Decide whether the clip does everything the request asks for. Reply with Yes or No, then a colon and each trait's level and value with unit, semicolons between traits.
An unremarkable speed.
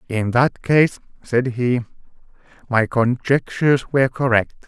No: slow, 115 wpm